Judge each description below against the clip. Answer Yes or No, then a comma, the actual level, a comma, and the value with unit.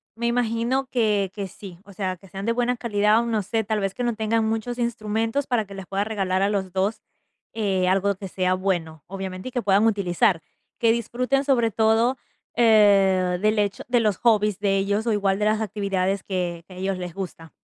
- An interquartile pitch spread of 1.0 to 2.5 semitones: No, average, 2.9 semitones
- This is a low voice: No, high, 205 Hz